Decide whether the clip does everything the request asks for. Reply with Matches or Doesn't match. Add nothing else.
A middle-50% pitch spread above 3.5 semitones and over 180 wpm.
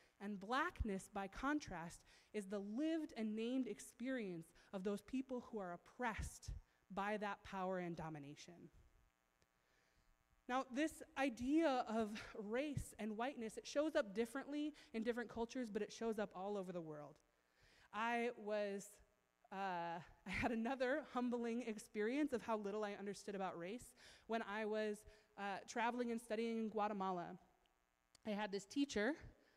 Doesn't match